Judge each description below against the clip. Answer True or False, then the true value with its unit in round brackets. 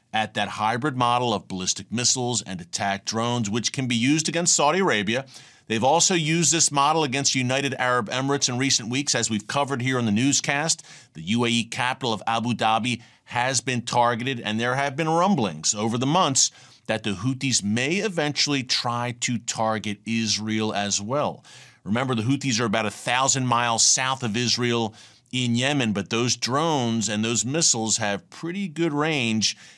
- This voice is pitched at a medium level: False (120 Hz)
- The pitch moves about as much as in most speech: True (3.8 semitones)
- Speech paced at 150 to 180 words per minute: True (175 wpm)